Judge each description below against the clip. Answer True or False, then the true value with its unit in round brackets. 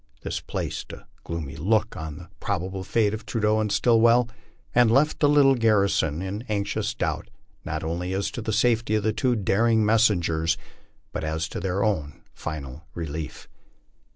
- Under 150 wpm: False (165 wpm)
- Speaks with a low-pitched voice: True (100 Hz)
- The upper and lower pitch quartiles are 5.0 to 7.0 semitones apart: True (5.3 semitones)